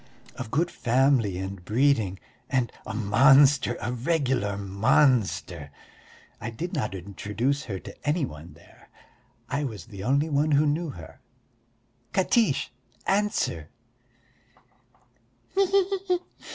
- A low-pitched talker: Yes, low, 125 Hz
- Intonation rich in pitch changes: Yes, wide, 6.3 semitones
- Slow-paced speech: Yes, slow, 110 wpm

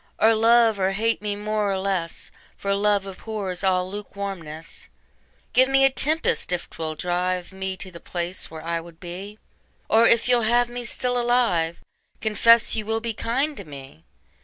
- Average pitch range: Yes, average, 4.3 semitones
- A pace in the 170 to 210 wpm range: Yes, average, 180 wpm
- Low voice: No, high, 200 Hz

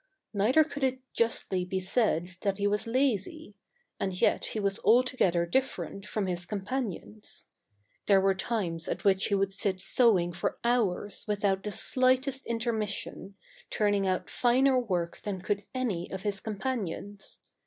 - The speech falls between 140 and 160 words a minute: Yes, average, 155 wpm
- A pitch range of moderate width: Yes, average, 4.0 semitones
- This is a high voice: Yes, high, 205 Hz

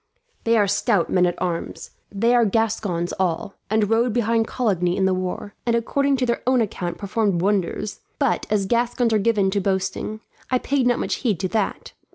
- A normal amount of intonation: Yes, average, 3.5 semitones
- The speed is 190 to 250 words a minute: Yes, average, 195 wpm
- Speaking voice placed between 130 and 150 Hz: No, high, 210 Hz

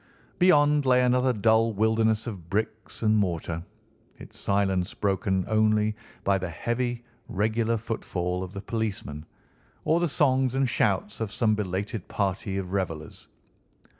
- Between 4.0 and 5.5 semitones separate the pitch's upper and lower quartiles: No, average, 3.4 semitones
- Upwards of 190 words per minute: No, slow, 135 wpm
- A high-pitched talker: No, low, 110 Hz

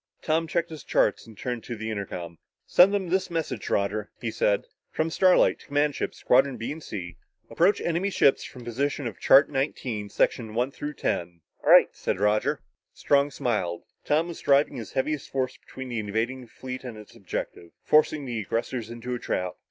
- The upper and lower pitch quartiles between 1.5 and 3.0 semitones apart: No, wide, 5.5 semitones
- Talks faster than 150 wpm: Yes, average, 185 wpm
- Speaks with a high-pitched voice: No, low, 125 Hz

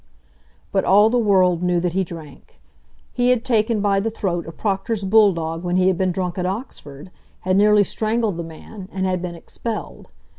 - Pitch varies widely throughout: No, average, 3.2 semitones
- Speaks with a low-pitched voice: No, high, 190 Hz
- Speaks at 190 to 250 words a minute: Yes, average, 195 wpm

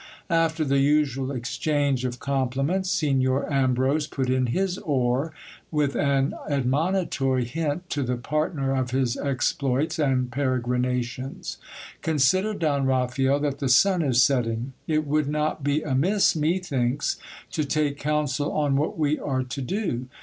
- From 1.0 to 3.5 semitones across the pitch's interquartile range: Yes, average, 2.9 semitones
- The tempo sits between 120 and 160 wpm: Yes, average, 140 wpm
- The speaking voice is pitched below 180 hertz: Yes, medium, 140 Hz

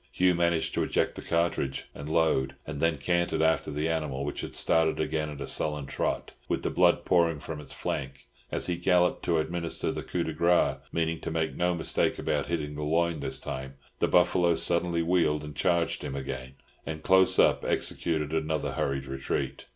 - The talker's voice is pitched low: Yes, very low, 80 Hz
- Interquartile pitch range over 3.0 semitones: No, narrow, 2.6 semitones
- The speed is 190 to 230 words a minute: Yes, average, 195 wpm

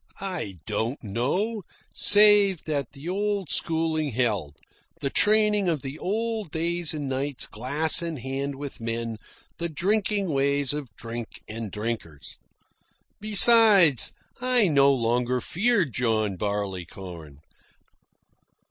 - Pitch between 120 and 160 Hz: Yes, medium, 140 Hz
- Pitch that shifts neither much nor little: No, wide, 8.5 semitones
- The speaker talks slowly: Yes, slow, 115 wpm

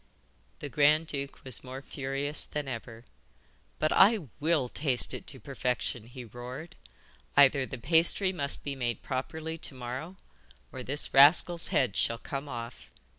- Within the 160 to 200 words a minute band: No, average, 150 wpm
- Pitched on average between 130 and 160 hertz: Yes, medium, 140 Hz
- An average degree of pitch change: Yes, average, 3.6 semitones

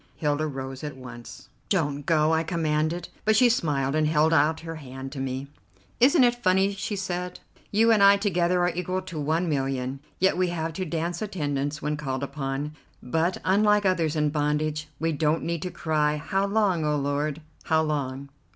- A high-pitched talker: No, medium, 155 Hz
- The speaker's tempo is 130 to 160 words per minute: No, average, 185 wpm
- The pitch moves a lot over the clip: No, average, 3.9 semitones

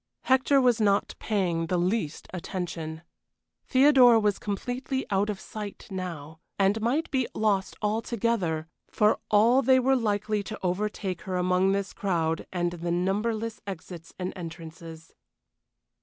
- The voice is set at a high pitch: Yes, high, 200 Hz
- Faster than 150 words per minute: No, slow, 135 wpm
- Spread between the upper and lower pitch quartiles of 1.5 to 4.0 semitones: No, average, 4.4 semitones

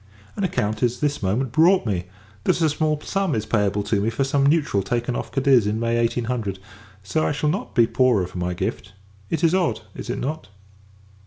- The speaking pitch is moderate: No, low, 120 Hz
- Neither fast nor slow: No, fast, 215 wpm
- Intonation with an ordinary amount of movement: No, wide, 6.1 semitones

